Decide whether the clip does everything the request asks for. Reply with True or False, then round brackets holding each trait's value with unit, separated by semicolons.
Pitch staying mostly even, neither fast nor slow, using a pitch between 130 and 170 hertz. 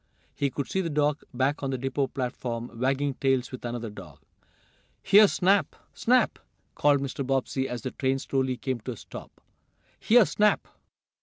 True (2.3 semitones; 165 wpm; 135 Hz)